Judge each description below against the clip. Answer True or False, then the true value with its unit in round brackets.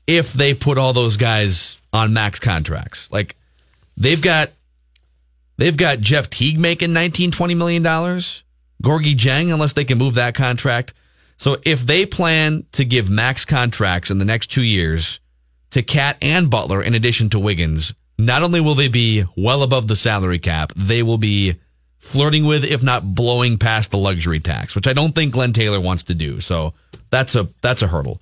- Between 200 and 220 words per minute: False (185 wpm)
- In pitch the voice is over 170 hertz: False (115 Hz)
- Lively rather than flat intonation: True (7.3 semitones)